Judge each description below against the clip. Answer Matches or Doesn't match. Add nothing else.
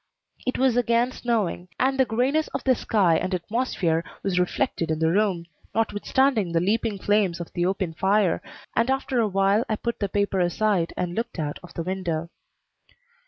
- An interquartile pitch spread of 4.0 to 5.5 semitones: Matches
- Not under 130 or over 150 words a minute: Doesn't match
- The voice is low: Doesn't match